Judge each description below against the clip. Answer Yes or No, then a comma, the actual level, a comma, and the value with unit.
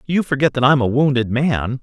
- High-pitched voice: No, low, 135 Hz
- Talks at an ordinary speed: No, fast, 230 wpm